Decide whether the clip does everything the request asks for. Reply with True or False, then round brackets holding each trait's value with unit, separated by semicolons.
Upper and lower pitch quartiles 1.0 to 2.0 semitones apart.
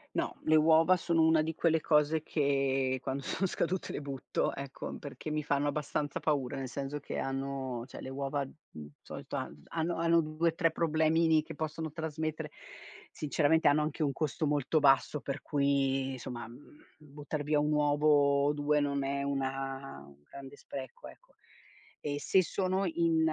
False (2.6 semitones)